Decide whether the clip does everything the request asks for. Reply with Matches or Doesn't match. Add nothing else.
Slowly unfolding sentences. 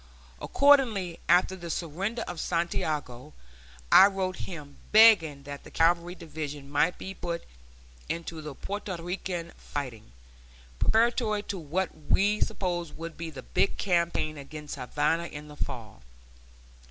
Matches